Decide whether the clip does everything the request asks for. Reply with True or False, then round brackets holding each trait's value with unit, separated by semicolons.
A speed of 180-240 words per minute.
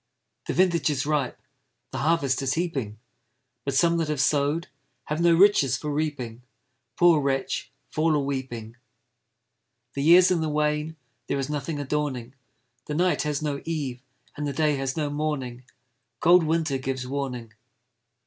False (155 wpm)